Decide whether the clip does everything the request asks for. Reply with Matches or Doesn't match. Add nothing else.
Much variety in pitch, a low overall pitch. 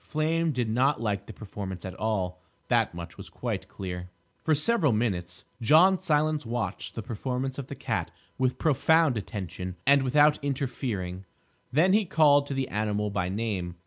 Matches